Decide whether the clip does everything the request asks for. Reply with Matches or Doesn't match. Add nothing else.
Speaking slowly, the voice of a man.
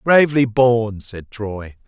Matches